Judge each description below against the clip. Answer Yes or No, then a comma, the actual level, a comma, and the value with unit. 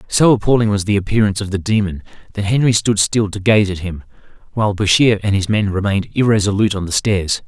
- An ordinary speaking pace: No, fast, 210 wpm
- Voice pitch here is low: Yes, low, 100 Hz